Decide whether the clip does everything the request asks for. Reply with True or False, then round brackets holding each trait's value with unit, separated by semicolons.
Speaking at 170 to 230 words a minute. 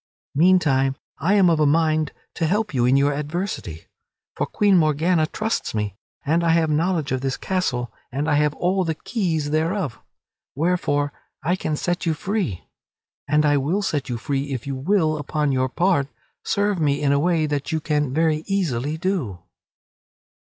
True (175 wpm)